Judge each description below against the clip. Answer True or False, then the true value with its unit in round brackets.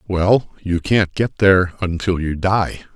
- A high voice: False (95 Hz)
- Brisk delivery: False (160 wpm)